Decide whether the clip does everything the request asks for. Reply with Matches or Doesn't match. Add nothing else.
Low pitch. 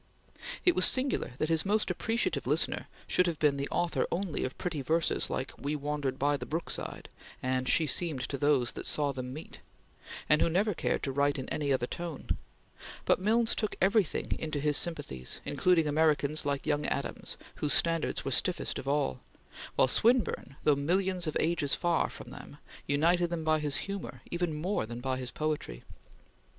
Doesn't match